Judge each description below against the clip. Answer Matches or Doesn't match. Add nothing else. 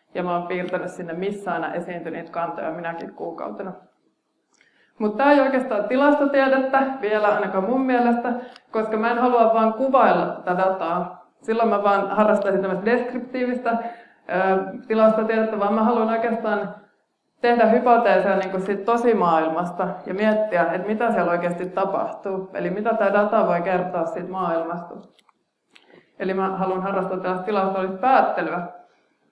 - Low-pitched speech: Doesn't match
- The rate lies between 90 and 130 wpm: Doesn't match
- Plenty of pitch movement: Doesn't match